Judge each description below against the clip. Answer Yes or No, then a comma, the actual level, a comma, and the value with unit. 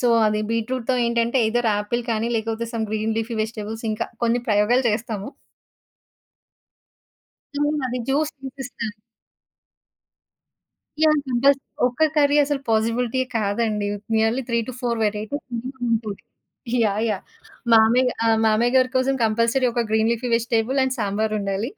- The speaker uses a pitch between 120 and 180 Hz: No, high, 230 Hz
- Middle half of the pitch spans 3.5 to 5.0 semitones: No, average, 2.7 semitones